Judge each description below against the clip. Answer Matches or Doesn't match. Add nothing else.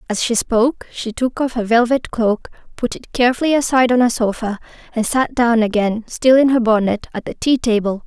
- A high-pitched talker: Matches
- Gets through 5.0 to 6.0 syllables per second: Matches